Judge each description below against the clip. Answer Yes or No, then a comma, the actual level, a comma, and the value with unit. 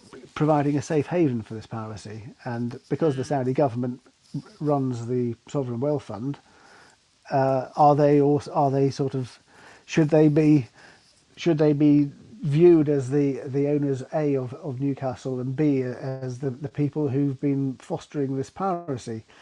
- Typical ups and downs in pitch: No, narrow, 2.2 semitones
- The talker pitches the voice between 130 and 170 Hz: Yes, medium, 140 Hz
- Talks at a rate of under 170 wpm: Yes, average, 160 wpm